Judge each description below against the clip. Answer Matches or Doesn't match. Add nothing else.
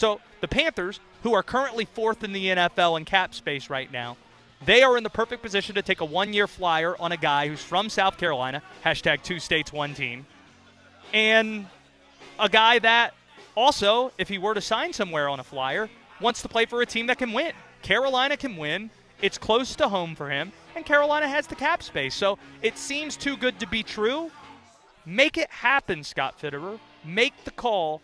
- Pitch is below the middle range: Doesn't match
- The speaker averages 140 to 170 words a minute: Doesn't match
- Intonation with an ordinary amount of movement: Doesn't match